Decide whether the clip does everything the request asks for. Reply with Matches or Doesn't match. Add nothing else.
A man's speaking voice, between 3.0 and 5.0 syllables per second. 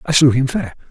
Doesn't match